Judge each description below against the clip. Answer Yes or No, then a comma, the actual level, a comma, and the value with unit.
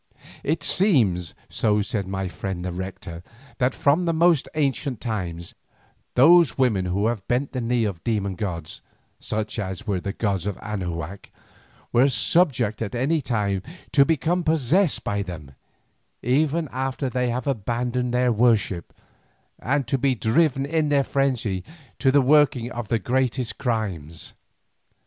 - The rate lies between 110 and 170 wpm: Yes, average, 150 wpm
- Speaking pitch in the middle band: No, low, 120 Hz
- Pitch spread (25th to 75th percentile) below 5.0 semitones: No, wide, 5.5 semitones